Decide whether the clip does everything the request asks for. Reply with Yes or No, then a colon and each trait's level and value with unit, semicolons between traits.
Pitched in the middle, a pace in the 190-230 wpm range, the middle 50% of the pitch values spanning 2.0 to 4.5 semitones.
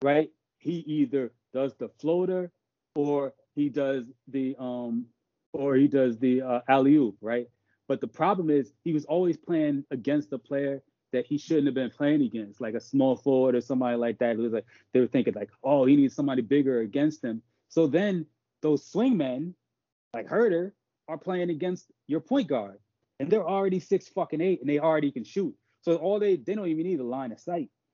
No: medium, 145 Hz; average, 200 wpm; average, 4.9 semitones